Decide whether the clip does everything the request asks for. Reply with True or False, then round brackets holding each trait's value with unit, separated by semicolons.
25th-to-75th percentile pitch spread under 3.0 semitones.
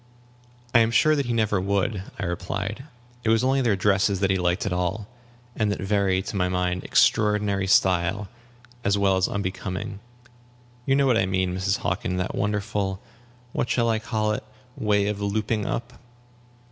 True (2.5 semitones)